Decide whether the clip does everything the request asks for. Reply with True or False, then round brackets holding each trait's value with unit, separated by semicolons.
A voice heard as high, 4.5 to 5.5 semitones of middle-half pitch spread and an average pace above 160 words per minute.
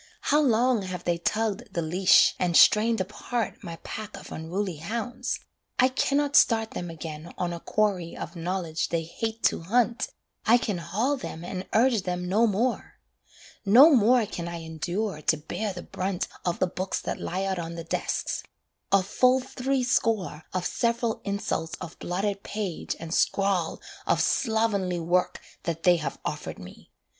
True (195 Hz; 4.8 semitones; 170 wpm)